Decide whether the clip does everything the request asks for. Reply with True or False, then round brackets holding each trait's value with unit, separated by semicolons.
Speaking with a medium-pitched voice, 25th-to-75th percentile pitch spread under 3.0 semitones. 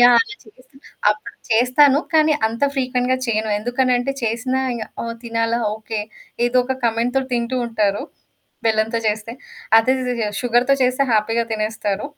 False (235 Hz; 2.4 semitones)